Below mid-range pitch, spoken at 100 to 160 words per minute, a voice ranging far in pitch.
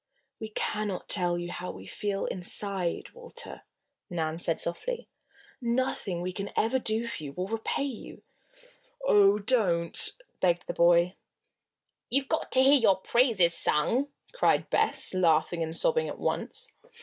No: high, 200 Hz; average, 150 wpm; wide, 6.0 semitones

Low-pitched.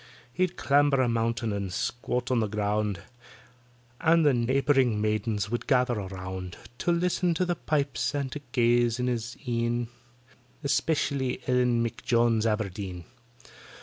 Yes: low, 120 Hz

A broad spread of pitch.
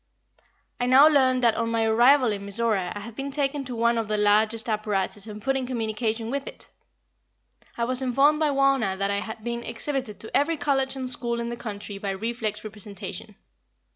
No: average, 3.7 semitones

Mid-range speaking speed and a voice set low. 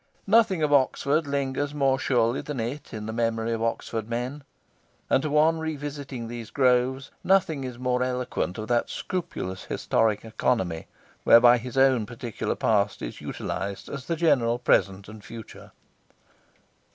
Yes: average, 150 wpm; low, 125 Hz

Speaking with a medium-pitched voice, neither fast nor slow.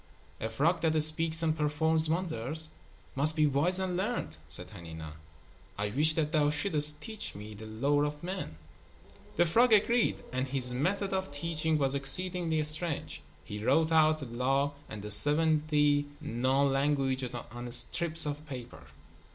Yes: medium, 150 Hz; average, 155 wpm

